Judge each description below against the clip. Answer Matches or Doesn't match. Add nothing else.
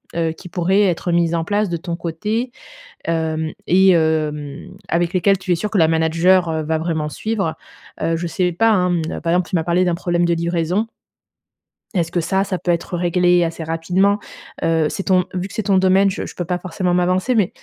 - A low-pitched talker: Doesn't match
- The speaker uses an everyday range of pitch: Doesn't match